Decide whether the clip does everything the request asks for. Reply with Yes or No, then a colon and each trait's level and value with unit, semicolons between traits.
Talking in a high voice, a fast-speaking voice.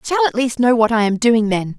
Yes: high, 225 Hz; fast, 335 wpm